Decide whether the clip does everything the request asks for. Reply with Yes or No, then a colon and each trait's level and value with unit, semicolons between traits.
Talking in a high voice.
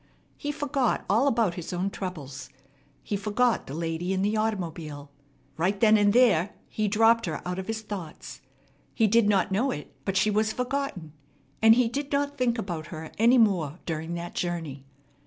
Yes: high, 205 Hz